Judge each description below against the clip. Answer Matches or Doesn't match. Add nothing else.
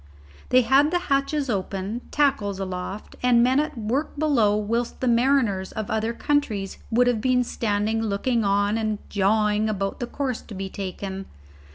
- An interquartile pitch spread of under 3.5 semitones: Doesn't match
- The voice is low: Doesn't match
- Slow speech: Doesn't match